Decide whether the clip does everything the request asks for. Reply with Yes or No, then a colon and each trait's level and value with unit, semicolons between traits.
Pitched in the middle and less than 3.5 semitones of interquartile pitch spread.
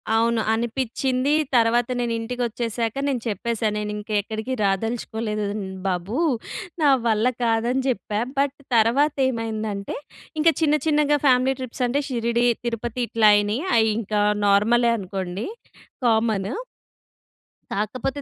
No: high, 230 Hz; average, 2.8 semitones